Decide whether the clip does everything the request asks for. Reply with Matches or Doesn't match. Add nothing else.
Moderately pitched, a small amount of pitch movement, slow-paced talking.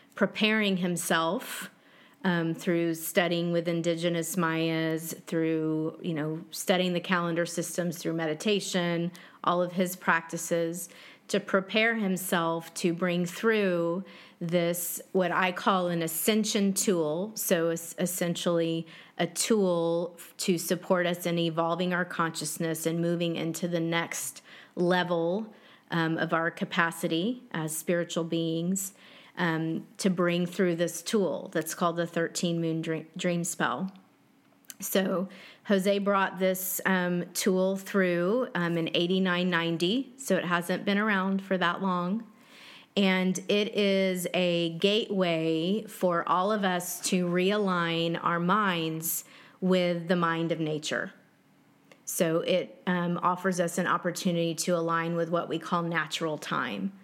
Matches